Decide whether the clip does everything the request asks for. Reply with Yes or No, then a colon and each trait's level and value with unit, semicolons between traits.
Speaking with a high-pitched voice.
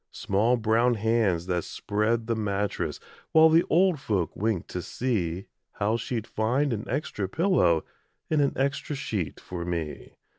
No: low, 110 Hz